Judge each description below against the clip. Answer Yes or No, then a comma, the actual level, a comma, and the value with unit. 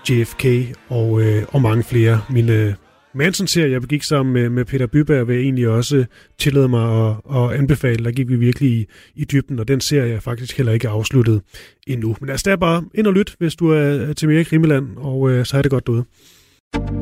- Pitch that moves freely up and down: No, average, 3.7 semitones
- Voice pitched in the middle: No, low, 130 Hz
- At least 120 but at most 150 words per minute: No, average, 220 wpm